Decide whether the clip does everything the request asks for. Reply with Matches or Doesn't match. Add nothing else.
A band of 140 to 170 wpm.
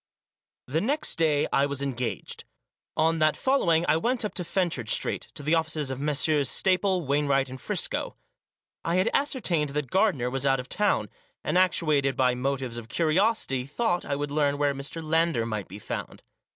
Doesn't match